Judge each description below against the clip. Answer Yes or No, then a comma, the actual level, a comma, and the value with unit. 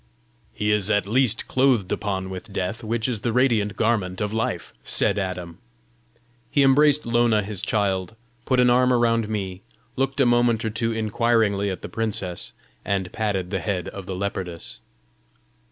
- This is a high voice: No, low, 105 Hz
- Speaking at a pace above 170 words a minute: No, average, 165 wpm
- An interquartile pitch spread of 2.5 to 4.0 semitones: Yes, average, 3.6 semitones